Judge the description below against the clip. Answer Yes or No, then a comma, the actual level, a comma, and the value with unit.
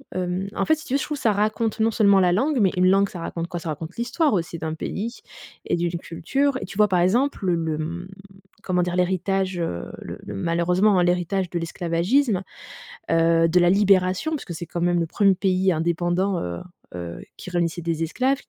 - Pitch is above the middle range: No, medium, 180 Hz